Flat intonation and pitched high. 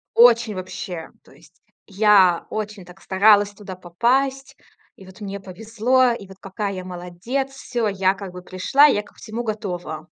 No: average, 3.7 semitones; high, 200 Hz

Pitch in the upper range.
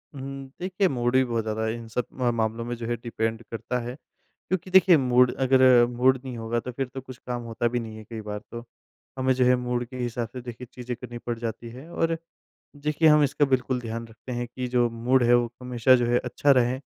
No: low, 125 Hz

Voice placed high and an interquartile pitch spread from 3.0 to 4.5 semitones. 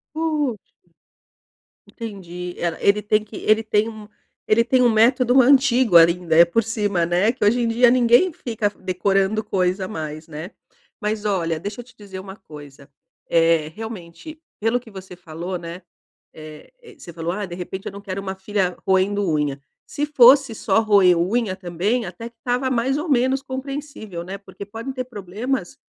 No: high, 205 Hz; average, 5.0 semitones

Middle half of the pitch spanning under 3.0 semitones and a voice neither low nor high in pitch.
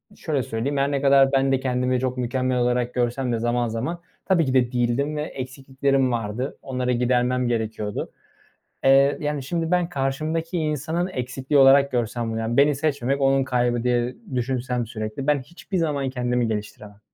No: narrow, 2.5 semitones; low, 130 Hz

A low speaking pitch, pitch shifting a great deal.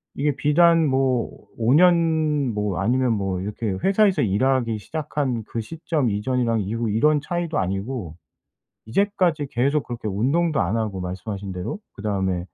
Yes: low, 120 Hz; wide, 6.6 semitones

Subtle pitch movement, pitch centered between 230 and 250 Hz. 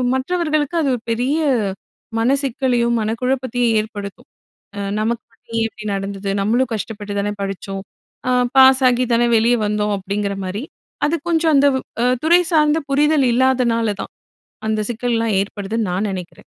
No: average, 4.1 semitones; high, 235 Hz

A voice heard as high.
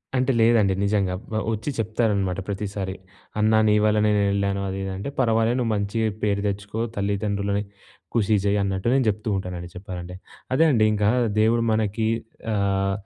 No: low, 100 Hz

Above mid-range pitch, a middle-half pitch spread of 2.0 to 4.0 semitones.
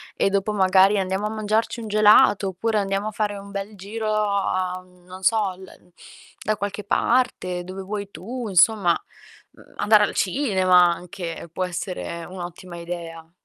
Yes: high, 195 Hz; narrow, 2.6 semitones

